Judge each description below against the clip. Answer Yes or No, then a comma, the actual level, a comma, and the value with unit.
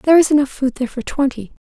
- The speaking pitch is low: No, very high, 270 Hz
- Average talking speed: No, fast, 250 wpm